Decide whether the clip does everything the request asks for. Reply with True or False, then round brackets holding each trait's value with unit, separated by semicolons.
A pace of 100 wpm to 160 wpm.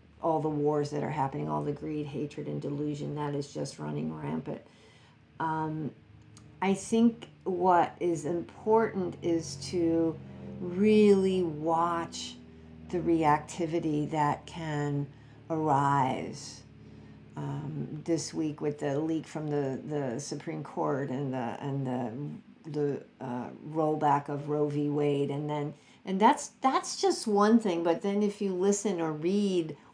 True (140 wpm)